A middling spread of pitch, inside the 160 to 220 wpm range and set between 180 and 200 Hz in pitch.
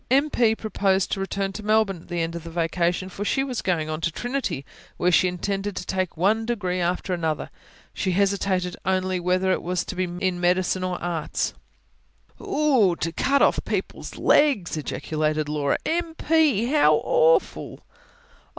Yes: average, 3.9 semitones; average, 170 wpm; medium, 185 Hz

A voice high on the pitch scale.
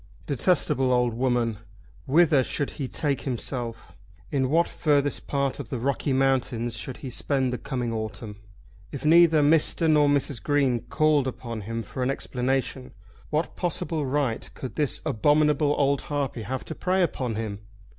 No: low, 135 Hz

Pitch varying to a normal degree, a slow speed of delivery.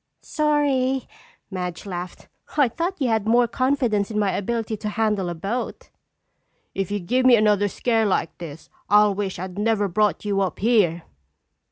No: average, 3.8 semitones; average, 165 wpm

